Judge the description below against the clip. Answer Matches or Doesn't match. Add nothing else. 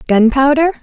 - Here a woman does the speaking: Matches